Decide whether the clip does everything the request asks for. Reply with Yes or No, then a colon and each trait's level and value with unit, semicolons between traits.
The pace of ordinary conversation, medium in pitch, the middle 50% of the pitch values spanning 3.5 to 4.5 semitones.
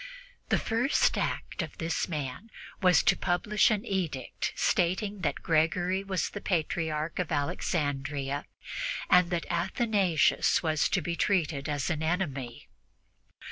No: slow, 130 wpm; medium, 170 Hz; average, 4.0 semitones